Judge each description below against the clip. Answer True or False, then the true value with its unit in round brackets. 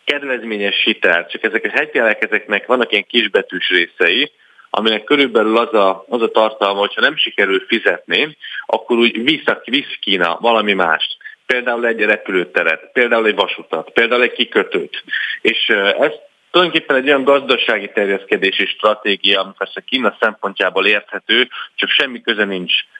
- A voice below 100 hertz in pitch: False (115 Hz)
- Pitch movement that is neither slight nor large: False (6.7 semitones)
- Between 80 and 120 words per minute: False (145 wpm)